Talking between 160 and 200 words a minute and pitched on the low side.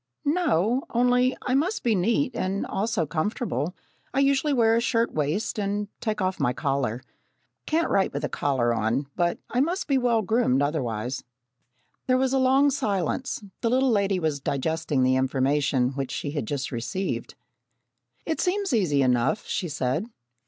No: average, 165 wpm; high, 190 Hz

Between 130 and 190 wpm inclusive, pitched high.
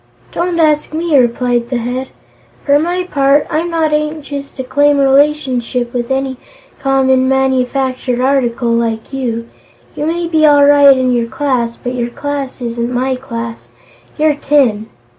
Yes: average, 150 wpm; very high, 265 Hz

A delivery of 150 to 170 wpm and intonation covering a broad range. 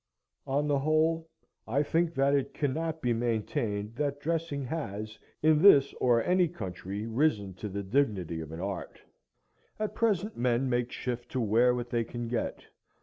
Yes: average, 165 wpm; wide, 5.8 semitones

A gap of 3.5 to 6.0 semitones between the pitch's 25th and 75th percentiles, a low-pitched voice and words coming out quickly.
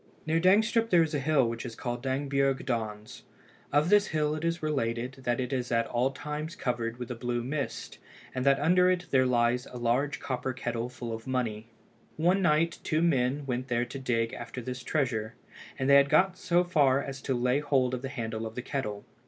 Yes: average, 3.9 semitones; low, 130 Hz; fast, 210 wpm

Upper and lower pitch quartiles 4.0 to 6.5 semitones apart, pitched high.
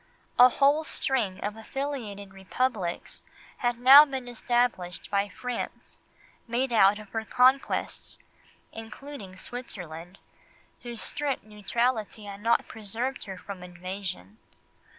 Yes: average, 4.3 semitones; high, 225 Hz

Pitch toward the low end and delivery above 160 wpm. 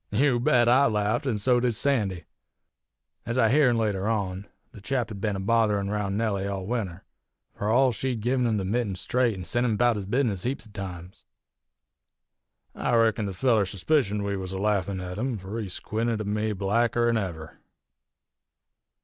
Yes: low, 105 Hz; average, 185 wpm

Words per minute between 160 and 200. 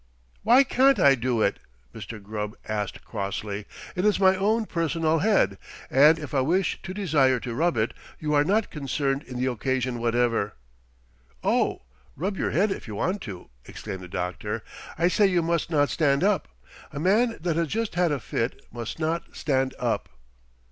Yes: average, 180 wpm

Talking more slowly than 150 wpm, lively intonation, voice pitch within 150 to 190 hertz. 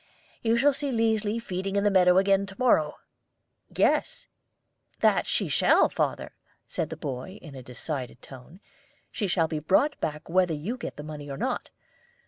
No: average, 170 wpm; wide, 5.9 semitones; medium, 185 Hz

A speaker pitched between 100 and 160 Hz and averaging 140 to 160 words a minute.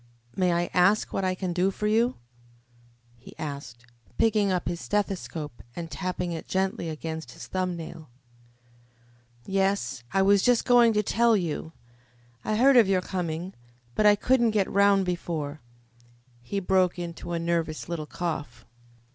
No: medium, 180 Hz; average, 155 wpm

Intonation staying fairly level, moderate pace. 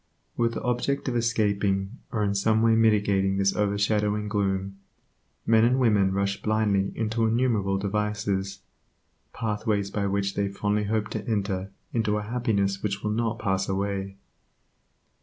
Yes: narrow, 2.0 semitones; average, 145 wpm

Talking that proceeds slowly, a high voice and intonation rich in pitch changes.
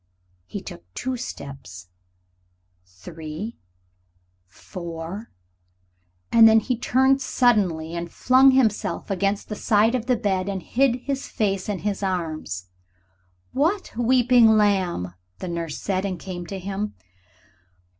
Yes: slow, 125 wpm; high, 200 Hz; wide, 5.8 semitones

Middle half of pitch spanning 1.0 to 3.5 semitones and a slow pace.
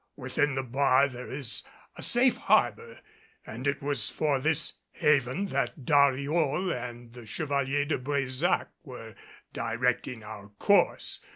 Yes: average, 2.9 semitones; slow, 130 wpm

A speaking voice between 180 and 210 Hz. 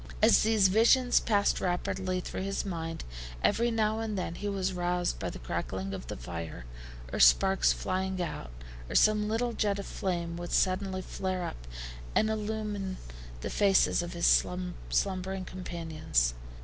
Yes: medium, 185 Hz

